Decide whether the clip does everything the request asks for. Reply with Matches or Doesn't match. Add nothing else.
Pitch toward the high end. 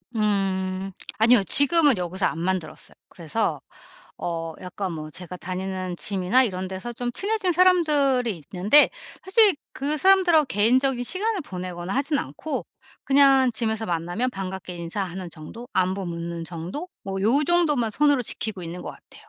Matches